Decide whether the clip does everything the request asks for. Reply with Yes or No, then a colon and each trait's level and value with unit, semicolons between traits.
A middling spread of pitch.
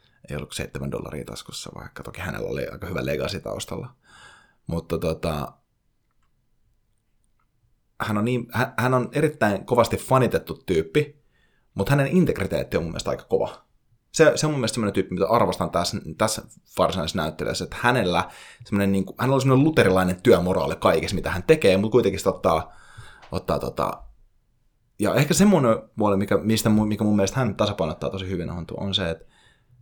Yes: average, 4.7 semitones